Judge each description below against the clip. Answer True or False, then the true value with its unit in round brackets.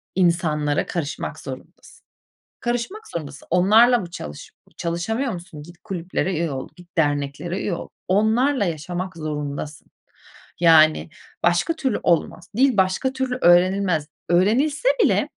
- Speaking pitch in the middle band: True (175 Hz)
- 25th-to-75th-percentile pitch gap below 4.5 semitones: False (5.6 semitones)